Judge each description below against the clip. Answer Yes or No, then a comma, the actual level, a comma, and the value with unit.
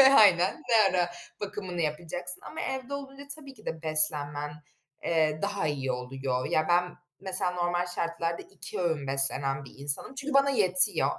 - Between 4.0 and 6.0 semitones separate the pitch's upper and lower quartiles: Yes, wide, 5.4 semitones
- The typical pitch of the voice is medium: Yes, medium, 175 Hz